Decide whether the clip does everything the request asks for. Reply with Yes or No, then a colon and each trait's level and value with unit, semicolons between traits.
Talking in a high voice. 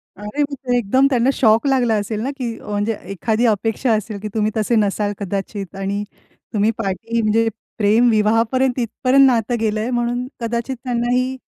Yes: high, 225 Hz